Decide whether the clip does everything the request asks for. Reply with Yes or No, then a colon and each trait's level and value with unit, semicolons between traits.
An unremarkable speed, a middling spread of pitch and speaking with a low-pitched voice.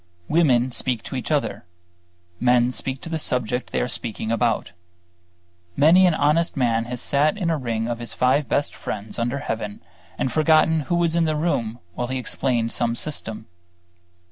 Yes: average, 175 wpm; average, 4.7 semitones; low, 130 Hz